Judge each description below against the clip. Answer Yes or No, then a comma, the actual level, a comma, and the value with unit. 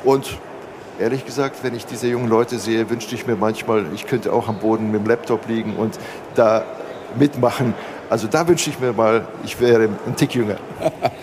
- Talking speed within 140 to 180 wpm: No, fast, 190 wpm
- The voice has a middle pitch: No, low, 115 Hz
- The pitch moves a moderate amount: No, narrow, 2.0 semitones